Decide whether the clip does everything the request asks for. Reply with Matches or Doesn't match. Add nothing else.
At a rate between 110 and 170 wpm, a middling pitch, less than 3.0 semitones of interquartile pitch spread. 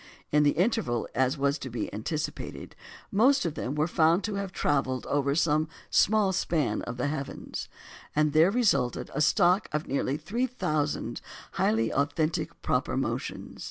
Doesn't match